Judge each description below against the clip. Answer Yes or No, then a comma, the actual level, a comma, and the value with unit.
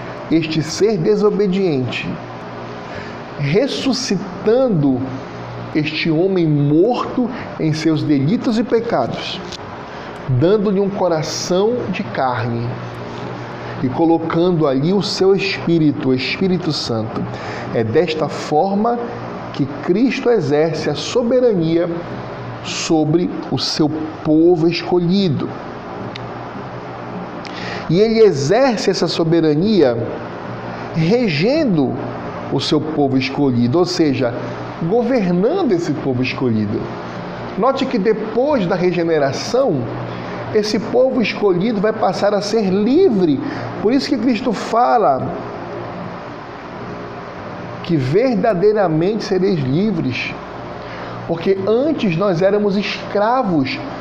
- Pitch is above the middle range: No, medium, 165 Hz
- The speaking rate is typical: No, slow, 90 wpm